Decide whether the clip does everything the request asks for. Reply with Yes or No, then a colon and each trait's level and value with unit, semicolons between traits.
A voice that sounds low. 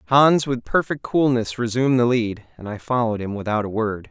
Yes: low, 120 Hz